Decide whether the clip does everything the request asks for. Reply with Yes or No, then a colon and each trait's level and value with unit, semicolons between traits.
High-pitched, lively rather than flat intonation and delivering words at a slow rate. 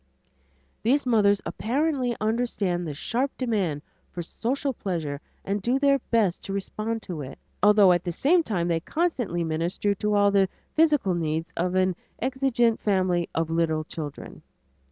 No: high, 200 Hz; wide, 5.9 semitones; average, 155 wpm